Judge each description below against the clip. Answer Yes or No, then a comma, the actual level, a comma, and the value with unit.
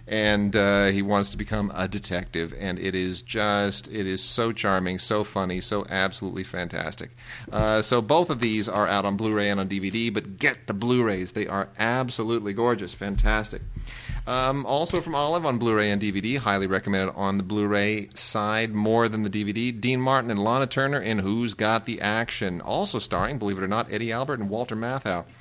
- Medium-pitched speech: No, low, 105 Hz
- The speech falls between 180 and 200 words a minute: Yes, average, 190 wpm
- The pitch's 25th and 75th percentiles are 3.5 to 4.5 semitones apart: No, average, 2.8 semitones